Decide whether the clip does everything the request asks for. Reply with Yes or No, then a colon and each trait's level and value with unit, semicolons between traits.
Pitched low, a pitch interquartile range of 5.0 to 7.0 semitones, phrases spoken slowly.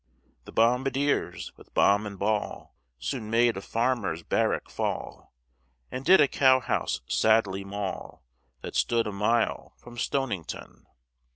No: low, 115 Hz; average, 4.1 semitones; slow, 130 wpm